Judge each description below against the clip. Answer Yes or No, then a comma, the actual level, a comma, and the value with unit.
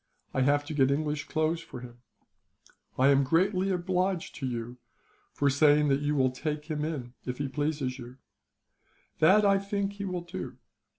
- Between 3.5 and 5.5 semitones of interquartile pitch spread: Yes, average, 4.5 semitones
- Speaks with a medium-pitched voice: Yes, medium, 150 Hz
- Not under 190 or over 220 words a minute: No, average, 170 wpm